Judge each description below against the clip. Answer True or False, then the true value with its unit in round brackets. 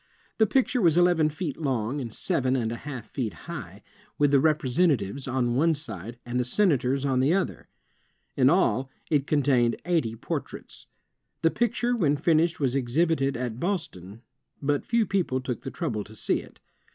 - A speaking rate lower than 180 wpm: True (170 wpm)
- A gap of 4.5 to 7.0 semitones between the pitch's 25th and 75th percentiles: True (5.0 semitones)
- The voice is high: False (140 Hz)